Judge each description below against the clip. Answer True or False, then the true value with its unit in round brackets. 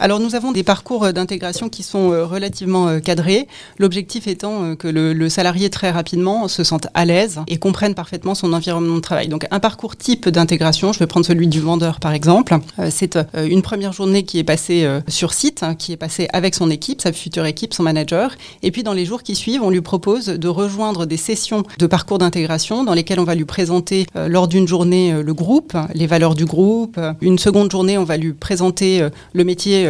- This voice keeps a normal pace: True (205 wpm)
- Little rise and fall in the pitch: False (3.1 semitones)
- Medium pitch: True (180 Hz)